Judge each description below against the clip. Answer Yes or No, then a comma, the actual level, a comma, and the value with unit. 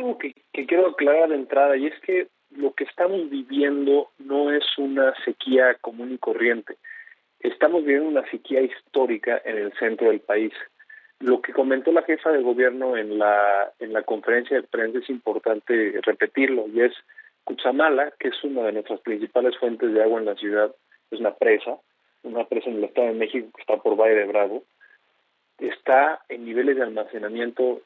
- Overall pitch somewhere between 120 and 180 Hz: Yes, medium, 140 Hz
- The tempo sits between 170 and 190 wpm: Yes, average, 175 wpm